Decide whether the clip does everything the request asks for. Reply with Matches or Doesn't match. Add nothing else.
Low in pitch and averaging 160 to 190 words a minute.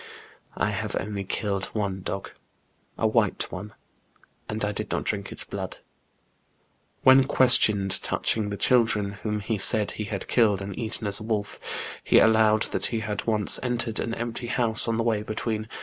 Matches